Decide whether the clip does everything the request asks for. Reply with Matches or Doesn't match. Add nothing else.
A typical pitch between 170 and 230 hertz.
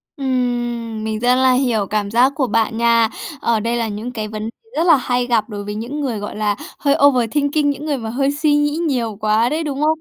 Doesn't match